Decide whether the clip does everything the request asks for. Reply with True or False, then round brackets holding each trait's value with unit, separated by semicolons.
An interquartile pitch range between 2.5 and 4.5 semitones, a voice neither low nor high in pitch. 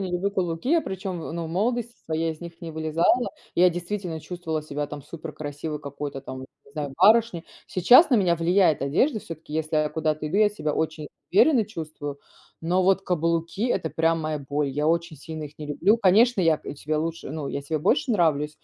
True (3.6 semitones; 165 Hz)